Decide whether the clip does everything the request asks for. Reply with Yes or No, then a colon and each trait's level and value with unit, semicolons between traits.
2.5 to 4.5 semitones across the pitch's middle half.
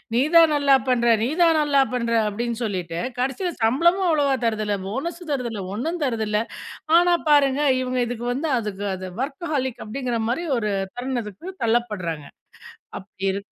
No: average, 5.1 semitones